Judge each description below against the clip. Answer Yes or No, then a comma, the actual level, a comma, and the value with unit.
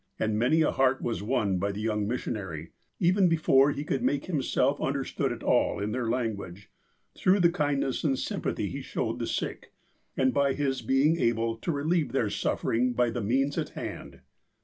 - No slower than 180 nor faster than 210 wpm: Yes, average, 185 wpm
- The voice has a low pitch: Yes, low, 130 Hz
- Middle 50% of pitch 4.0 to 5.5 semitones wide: Yes, average, 4.3 semitones